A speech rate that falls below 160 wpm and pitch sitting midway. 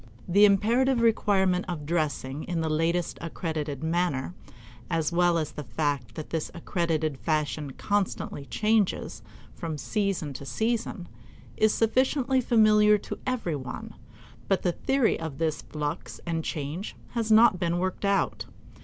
Yes: average, 140 wpm; medium, 175 Hz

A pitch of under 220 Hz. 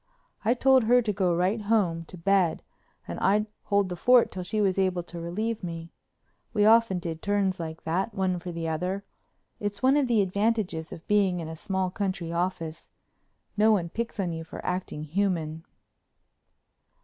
Yes: medium, 185 Hz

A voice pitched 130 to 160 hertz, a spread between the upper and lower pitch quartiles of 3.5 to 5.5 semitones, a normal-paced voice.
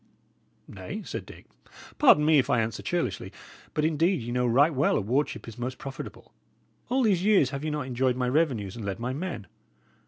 Yes: low, 135 Hz; average, 4.4 semitones; average, 195 wpm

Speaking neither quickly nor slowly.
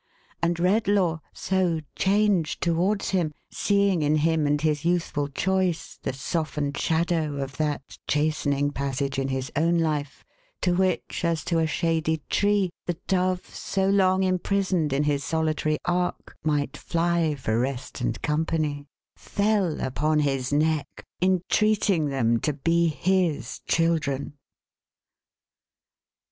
No: slow, 130 wpm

